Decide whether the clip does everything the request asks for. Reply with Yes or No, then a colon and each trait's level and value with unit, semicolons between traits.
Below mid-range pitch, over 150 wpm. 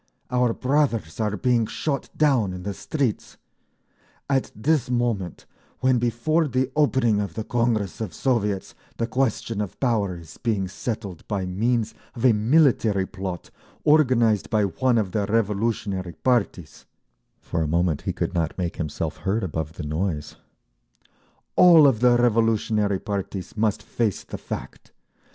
No: low, 110 Hz; average, 145 wpm